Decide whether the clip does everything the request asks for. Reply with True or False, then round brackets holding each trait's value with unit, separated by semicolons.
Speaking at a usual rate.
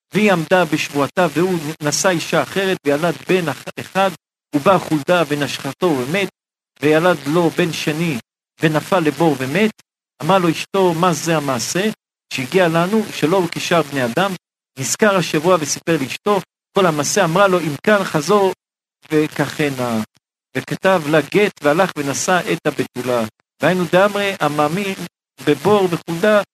True (130 wpm)